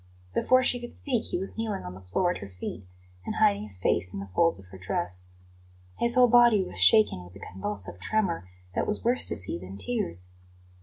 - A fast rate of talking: Yes, fast, 215 wpm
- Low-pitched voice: Yes, low, 100 Hz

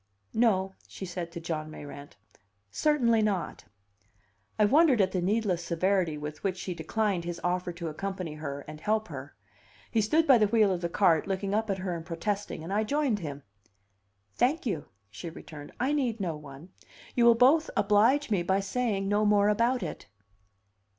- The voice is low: No, high, 195 Hz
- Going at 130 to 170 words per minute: No, average, 180 wpm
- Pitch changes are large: No, average, 4.6 semitones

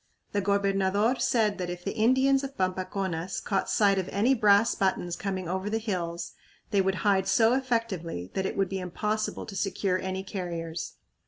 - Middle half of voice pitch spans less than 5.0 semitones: Yes, narrow, 2.5 semitones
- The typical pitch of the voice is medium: No, high, 195 Hz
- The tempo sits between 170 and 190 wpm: Yes, average, 175 wpm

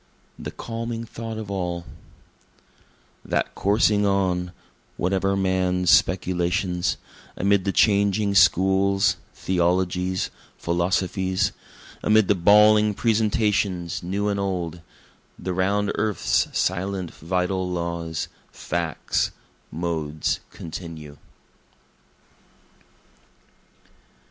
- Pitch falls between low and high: No, very low, 95 Hz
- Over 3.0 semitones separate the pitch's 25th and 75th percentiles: No, narrow, 2.4 semitones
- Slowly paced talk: Yes, slow, 80 wpm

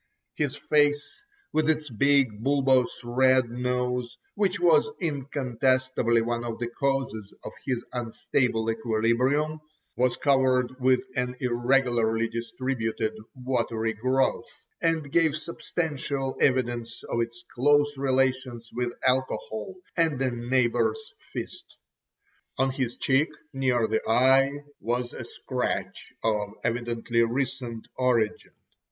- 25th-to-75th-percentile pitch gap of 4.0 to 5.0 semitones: No, average, 2.7 semitones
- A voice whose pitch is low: Yes, low, 125 Hz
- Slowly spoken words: Yes, slow, 110 wpm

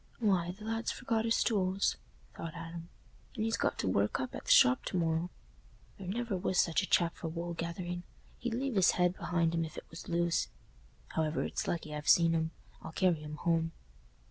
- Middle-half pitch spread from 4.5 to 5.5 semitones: No, average, 2.8 semitones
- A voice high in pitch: No, medium, 175 Hz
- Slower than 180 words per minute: No, average, 200 wpm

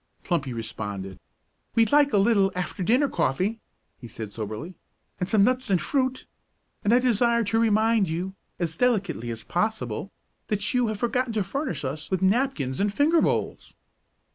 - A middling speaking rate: Yes, average, 165 wpm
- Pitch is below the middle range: No, high, 200 Hz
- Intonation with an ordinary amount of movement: No, wide, 6.6 semitones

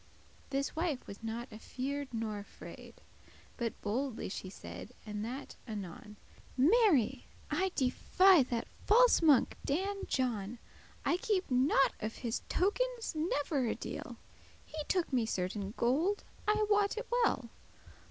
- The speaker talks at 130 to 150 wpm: Yes, average, 140 wpm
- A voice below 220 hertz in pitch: No, very high, 270 Hz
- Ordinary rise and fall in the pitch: No, wide, 8.5 semitones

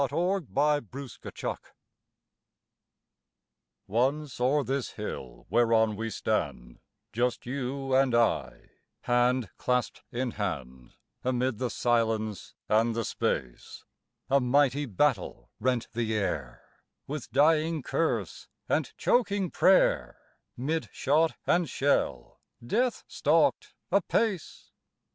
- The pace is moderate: No, slow, 105 wpm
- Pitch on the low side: Yes, low, 125 Hz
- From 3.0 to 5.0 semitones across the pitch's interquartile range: Yes, average, 4.5 semitones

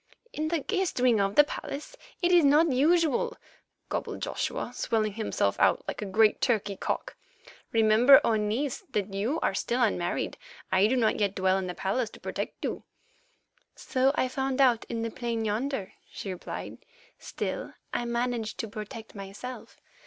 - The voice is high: Yes, high, 230 Hz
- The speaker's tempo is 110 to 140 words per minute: No, average, 165 wpm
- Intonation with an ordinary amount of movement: Yes, average, 4.3 semitones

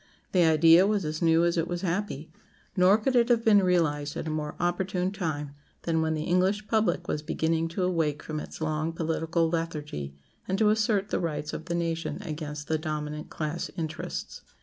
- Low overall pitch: No, medium, 165 Hz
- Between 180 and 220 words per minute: Yes, average, 195 wpm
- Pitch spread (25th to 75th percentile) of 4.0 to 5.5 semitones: No, average, 2.9 semitones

